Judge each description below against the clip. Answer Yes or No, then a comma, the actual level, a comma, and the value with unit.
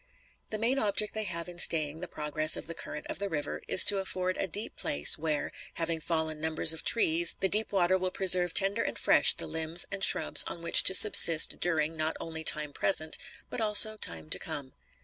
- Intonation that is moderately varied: Yes, average, 3.5 semitones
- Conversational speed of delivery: No, fast, 210 wpm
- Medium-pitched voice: Yes, medium, 170 Hz